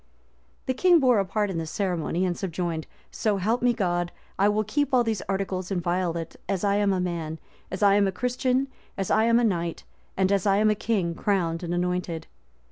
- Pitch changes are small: No, average, 3.6 semitones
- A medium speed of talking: No, fast, 210 wpm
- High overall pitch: Yes, high, 195 Hz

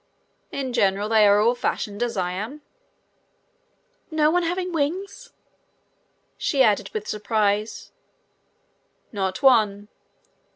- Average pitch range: No, wide, 6.2 semitones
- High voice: Yes, high, 220 Hz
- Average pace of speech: No, slow, 110 wpm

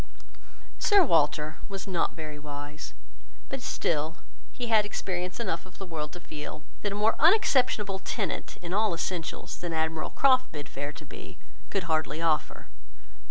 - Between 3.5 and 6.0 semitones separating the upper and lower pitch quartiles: Yes, average, 4.9 semitones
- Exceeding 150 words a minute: Yes, average, 160 wpm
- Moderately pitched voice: Yes, medium, 170 Hz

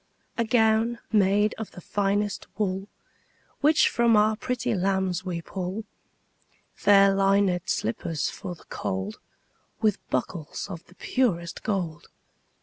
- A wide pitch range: No, average, 3.4 semitones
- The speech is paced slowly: Yes, slow, 130 wpm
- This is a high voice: Yes, high, 195 Hz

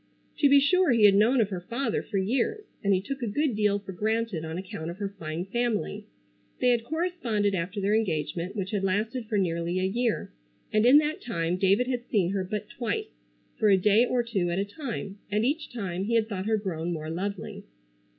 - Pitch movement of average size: Yes, average, 4.1 semitones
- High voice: Yes, high, 205 Hz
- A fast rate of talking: Yes, fast, 220 wpm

